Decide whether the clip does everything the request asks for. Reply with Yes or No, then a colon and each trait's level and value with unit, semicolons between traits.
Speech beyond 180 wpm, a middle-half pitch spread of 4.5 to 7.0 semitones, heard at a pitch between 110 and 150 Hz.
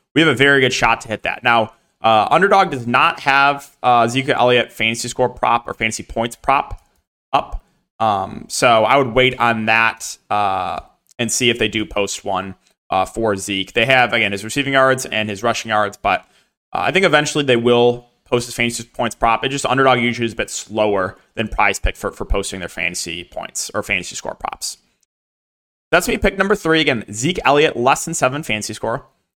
No: fast, 205 wpm; average, 3.4 semitones; low, 120 Hz